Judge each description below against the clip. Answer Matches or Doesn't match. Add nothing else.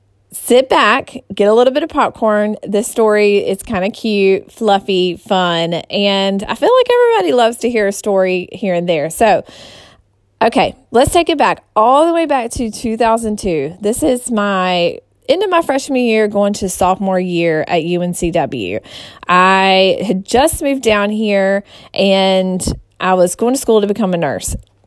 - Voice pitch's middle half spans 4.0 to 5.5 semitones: Matches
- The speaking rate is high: Doesn't match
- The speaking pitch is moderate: Doesn't match